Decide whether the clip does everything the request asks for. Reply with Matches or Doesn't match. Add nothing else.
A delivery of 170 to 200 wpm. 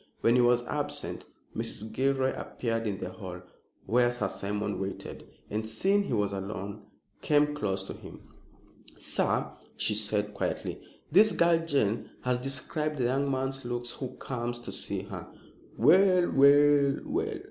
Doesn't match